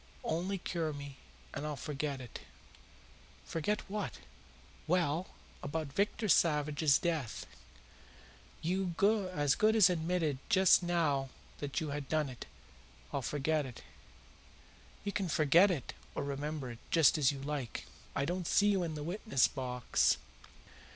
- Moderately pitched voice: Yes, medium, 155 Hz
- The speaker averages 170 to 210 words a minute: No, slow, 135 wpm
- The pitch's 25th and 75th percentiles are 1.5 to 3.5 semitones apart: No, average, 4.0 semitones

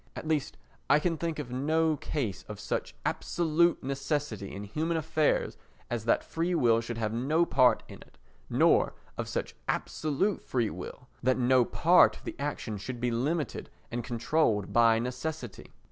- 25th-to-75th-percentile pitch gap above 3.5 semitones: Yes, average, 5.3 semitones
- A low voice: Yes, low, 130 Hz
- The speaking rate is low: No, average, 165 wpm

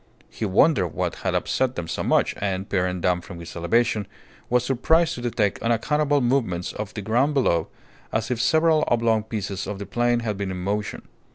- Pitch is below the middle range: Yes, low, 110 Hz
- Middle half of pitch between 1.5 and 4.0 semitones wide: No, average, 4.4 semitones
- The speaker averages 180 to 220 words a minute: Yes, average, 190 wpm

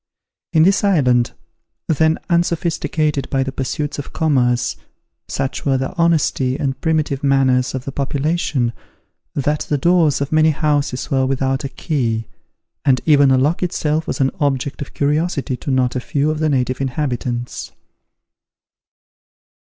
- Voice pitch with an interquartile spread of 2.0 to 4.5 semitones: Yes, average, 2.9 semitones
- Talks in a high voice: No, medium, 140 Hz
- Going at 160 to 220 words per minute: No, average, 145 wpm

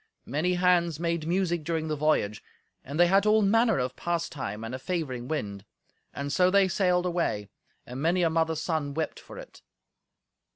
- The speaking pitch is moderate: Yes, medium, 165 Hz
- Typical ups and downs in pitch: Yes, average, 4.1 semitones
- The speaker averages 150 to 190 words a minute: Yes, average, 175 wpm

